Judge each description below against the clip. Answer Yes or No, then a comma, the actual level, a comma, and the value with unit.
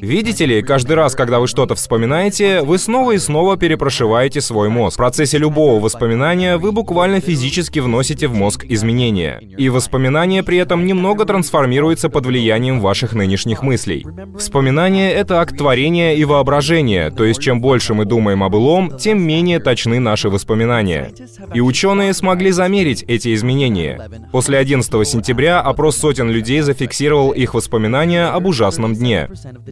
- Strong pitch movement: Yes, wide, 6.5 semitones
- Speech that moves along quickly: No, average, 150 wpm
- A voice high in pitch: No, low, 135 Hz